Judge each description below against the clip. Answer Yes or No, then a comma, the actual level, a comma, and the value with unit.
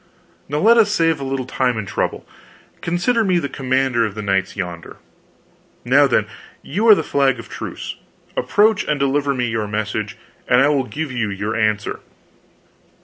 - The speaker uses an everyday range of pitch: No, wide, 6.6 semitones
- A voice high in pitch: No, low, 135 Hz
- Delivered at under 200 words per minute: Yes, average, 175 wpm